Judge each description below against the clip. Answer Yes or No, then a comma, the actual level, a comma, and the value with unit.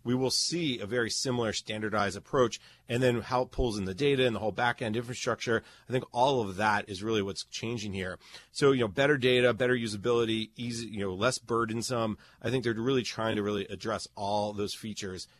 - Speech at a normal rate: No, fast, 210 wpm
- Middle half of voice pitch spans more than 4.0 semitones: No, average, 3.3 semitones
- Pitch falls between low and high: No, low, 115 Hz